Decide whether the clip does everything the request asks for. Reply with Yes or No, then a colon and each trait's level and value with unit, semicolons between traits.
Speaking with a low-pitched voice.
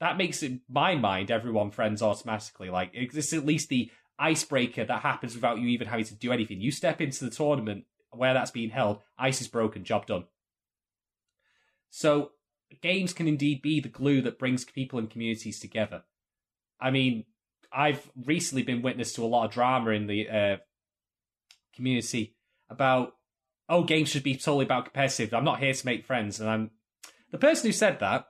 Yes: low, 125 Hz